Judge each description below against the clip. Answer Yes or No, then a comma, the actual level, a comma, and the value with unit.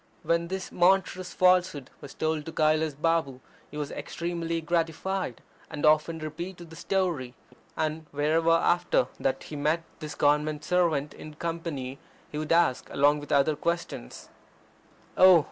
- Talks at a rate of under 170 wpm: Yes, average, 145 wpm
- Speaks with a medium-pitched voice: Yes, medium, 160 Hz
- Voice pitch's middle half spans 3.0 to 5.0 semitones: No, narrow, 2.5 semitones